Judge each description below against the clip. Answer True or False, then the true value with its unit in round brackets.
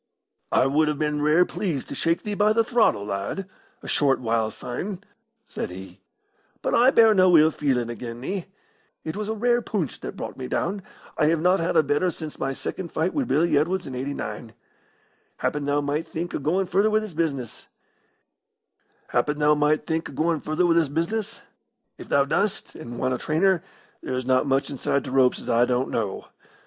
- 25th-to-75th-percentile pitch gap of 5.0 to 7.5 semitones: True (5.5 semitones)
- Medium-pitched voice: True (155 Hz)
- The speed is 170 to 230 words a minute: True (175 wpm)